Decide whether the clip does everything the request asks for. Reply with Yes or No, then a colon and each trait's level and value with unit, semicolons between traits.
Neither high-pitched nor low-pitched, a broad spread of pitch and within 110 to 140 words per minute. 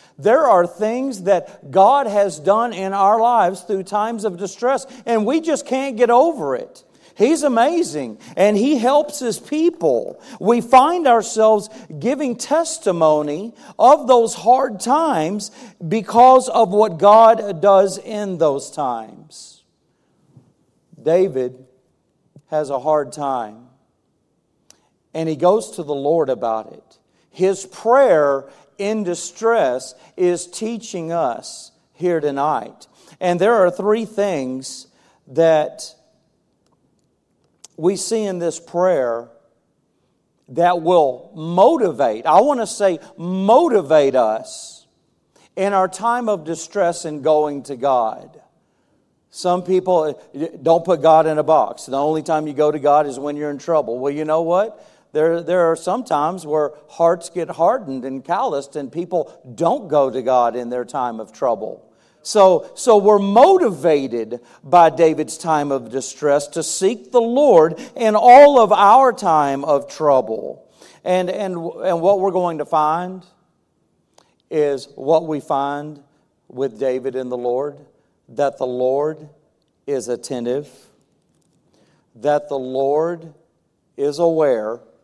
Yes: medium, 170 Hz; wide, 6.4 semitones; slow, 135 wpm